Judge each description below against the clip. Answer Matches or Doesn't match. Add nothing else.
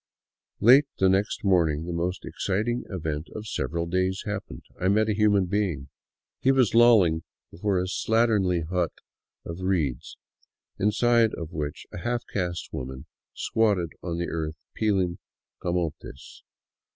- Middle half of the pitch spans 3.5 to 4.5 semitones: Matches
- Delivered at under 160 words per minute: Matches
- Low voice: Matches